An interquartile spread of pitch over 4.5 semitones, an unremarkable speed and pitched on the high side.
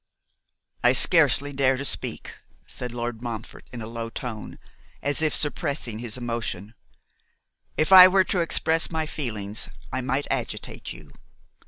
No: average, 5.0 semitones; average, 145 wpm; low, 130 Hz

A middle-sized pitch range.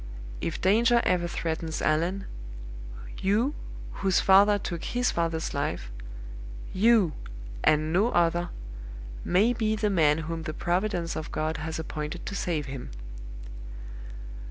Yes: average, 4.2 semitones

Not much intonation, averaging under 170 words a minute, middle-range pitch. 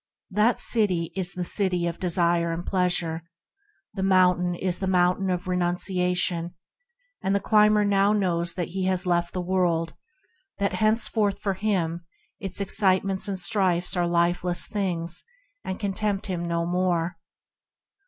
Yes: narrow, 2.1 semitones; average, 145 wpm; medium, 180 Hz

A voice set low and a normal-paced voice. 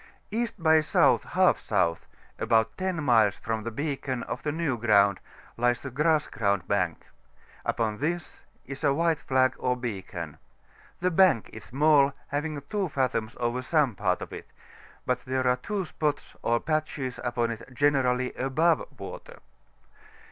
Yes: low, 130 Hz; average, 155 wpm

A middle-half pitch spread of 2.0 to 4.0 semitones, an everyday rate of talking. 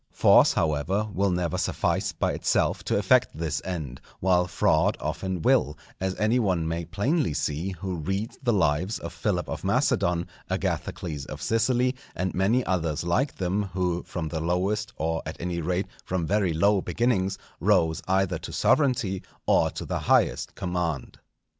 Yes: average, 3.5 semitones; average, 160 wpm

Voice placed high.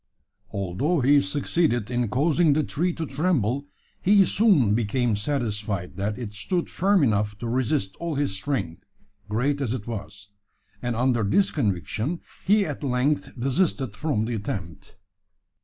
No: low, 125 Hz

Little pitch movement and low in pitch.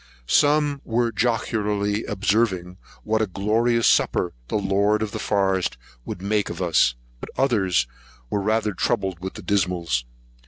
No: average, 3.0 semitones; low, 105 Hz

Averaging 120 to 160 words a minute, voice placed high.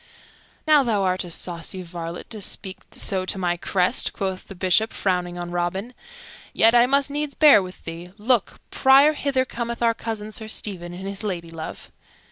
No: average, 175 wpm; high, 195 Hz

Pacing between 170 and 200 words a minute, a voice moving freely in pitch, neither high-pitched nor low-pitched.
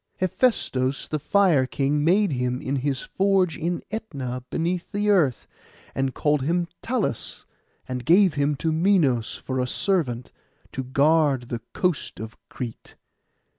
No: average, 140 wpm; wide, 5.7 semitones; medium, 150 Hz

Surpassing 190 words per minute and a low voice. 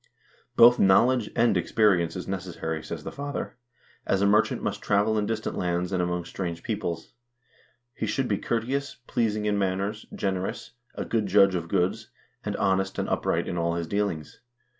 No: average, 180 wpm; low, 100 Hz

